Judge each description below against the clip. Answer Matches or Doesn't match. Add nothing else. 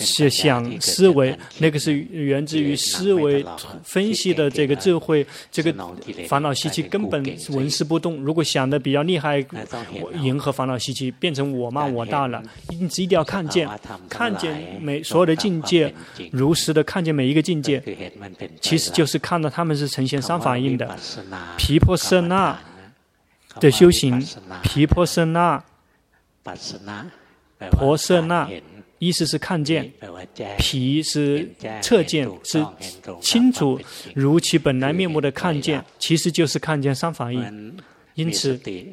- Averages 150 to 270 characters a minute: Matches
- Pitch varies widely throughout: Doesn't match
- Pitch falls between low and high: Matches